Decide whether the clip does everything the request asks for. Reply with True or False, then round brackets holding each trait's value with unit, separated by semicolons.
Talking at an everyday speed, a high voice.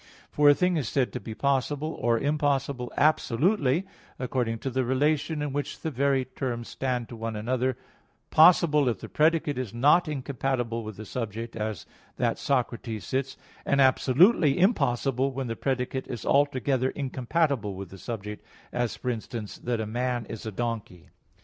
False (165 wpm; 130 Hz)